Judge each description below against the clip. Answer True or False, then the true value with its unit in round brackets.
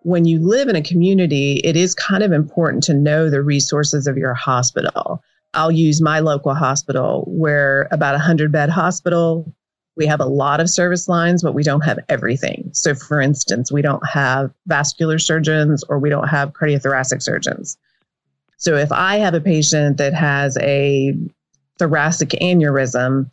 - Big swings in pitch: False (2.8 semitones)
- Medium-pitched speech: True (150 Hz)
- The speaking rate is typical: True (170 wpm)